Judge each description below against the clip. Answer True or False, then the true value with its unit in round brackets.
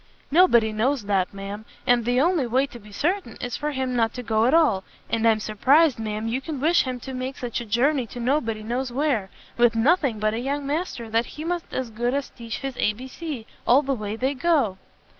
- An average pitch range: True (3.9 semitones)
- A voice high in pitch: True (245 Hz)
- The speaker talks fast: True (230 wpm)